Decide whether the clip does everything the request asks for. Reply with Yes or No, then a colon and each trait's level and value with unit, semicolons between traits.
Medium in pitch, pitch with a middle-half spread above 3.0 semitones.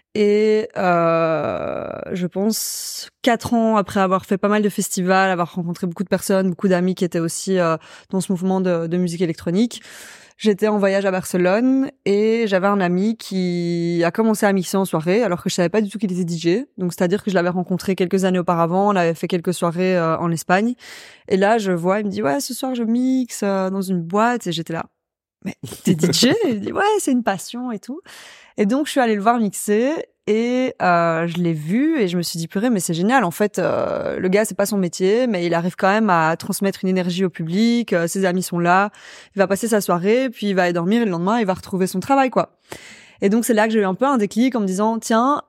No: high, 195 Hz; average, 3.7 semitones